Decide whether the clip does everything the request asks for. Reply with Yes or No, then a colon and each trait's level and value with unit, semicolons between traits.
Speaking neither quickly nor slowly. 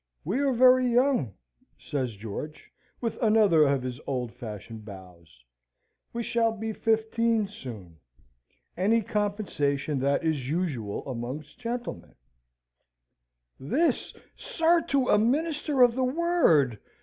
No: slow, 115 wpm